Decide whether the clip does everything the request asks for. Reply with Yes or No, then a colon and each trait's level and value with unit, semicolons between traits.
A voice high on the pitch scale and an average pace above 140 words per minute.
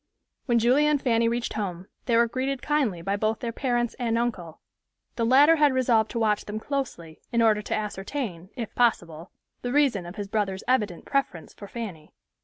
Yes: high, 230 Hz; average, 190 wpm